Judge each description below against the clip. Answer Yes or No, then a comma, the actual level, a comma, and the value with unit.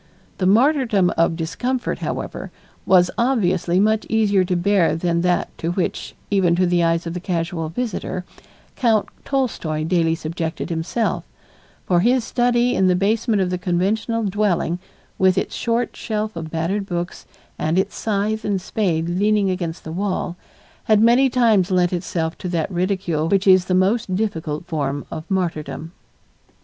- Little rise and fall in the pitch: No, average, 3.9 semitones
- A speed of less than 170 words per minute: Yes, average, 160 wpm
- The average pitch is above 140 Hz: Yes, medium, 185 Hz